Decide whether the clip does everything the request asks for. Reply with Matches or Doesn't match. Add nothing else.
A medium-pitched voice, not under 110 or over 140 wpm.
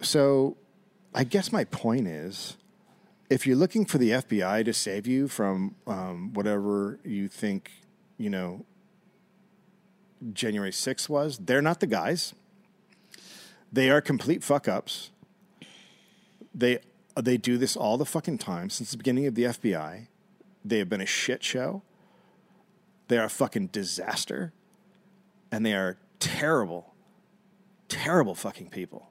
Matches